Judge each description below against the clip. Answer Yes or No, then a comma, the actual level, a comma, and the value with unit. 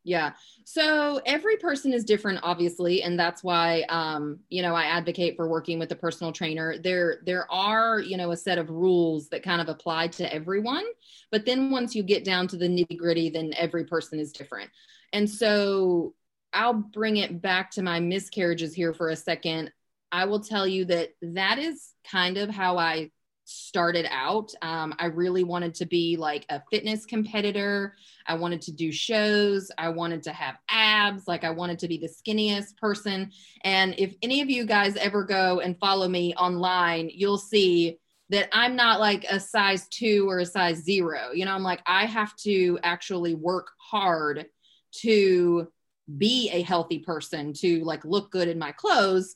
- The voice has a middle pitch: Yes, medium, 180 Hz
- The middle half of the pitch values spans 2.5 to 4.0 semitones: Yes, average, 3.3 semitones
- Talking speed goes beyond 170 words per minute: Yes, average, 185 wpm